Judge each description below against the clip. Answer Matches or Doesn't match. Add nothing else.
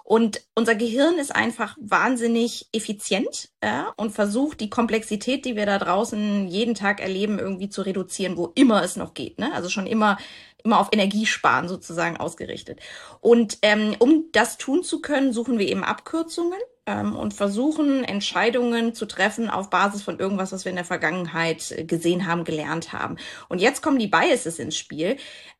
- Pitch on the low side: Doesn't match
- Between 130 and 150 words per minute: Doesn't match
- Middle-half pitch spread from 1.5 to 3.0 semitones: Doesn't match